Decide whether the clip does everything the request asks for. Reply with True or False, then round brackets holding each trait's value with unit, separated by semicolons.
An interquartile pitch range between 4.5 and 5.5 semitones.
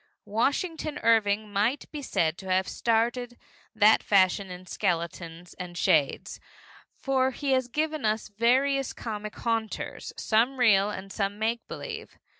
True (4.8 semitones)